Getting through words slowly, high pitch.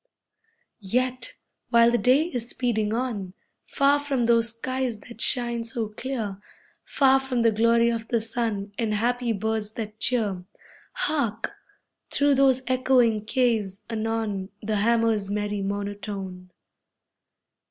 Yes: slow, 125 wpm; high, 230 Hz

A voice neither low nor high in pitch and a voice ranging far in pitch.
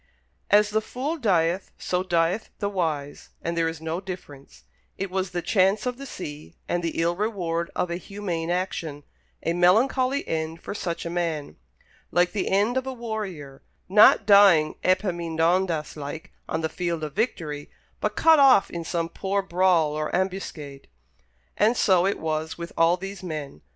No: medium, 175 Hz; average, 3.5 semitones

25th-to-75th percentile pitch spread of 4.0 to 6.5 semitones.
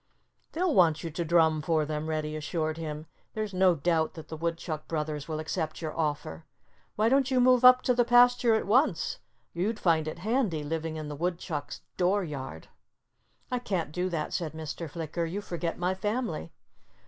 Yes: average, 4.7 semitones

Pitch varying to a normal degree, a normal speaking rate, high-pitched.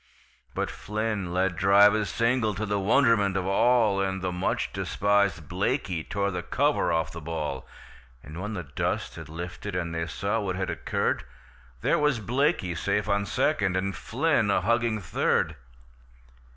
No: average, 3.4 semitones; average, 165 wpm; low, 100 Hz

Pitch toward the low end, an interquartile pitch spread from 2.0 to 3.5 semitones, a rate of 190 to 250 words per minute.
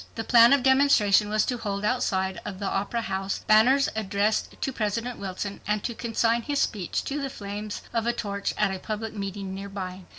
No: high, 210 Hz; average, 2.9 semitones; average, 195 wpm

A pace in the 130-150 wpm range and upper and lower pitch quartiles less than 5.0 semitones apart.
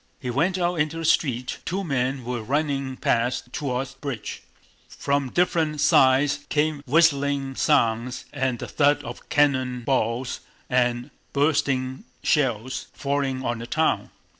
Yes: average, 140 wpm; average, 2.8 semitones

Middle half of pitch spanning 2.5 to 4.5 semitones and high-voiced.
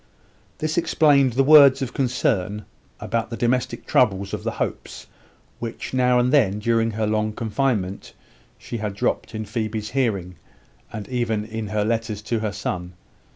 No: average, 3.1 semitones; low, 115 Hz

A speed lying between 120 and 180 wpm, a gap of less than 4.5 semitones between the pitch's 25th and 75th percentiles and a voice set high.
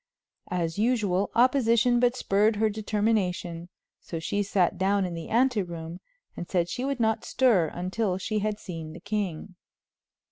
Yes: average, 155 wpm; average, 4.1 semitones; high, 205 Hz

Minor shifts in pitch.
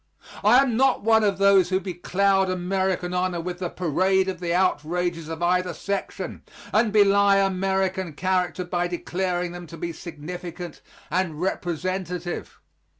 Yes: narrow, 1.7 semitones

